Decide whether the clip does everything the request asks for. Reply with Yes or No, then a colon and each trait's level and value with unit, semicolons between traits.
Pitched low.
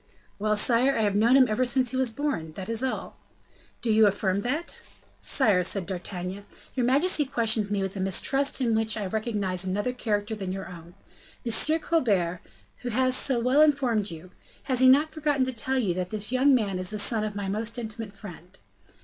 No: high, 220 Hz